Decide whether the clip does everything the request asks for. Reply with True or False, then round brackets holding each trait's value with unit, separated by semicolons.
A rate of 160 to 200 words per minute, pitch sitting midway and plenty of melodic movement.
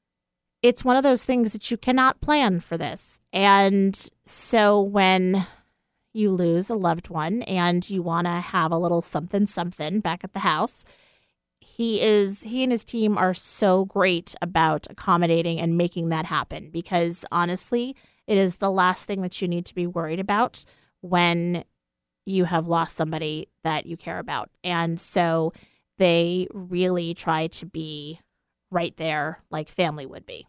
False (165 wpm; 180 Hz; 3.2 semitones)